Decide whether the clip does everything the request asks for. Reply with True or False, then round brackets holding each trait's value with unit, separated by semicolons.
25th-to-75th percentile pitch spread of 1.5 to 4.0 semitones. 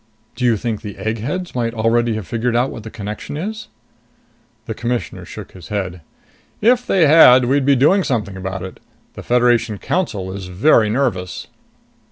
False (4.7 semitones)